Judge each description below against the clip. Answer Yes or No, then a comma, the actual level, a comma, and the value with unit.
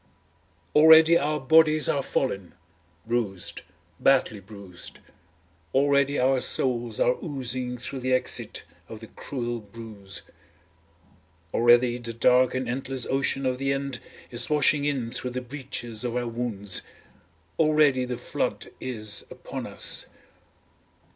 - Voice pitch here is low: Yes, low, 125 Hz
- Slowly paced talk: Yes, slow, 125 wpm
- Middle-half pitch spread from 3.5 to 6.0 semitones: No, average, 2.8 semitones